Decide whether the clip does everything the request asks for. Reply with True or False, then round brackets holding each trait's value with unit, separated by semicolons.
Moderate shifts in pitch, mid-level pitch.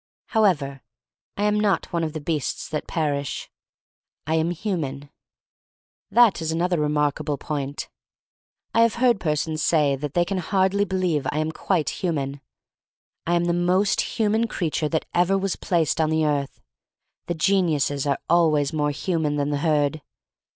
True (3.9 semitones; 160 Hz)